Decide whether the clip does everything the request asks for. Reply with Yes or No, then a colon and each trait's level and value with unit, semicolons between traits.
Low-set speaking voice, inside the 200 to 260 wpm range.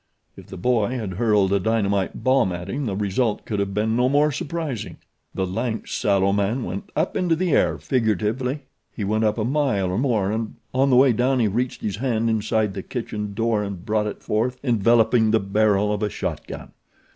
Yes: low, 110 Hz; fast, 205 wpm